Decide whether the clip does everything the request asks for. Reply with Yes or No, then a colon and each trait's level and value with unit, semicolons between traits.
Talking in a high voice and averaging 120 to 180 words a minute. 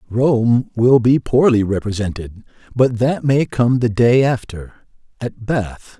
No: low, 120 Hz; average, 140 wpm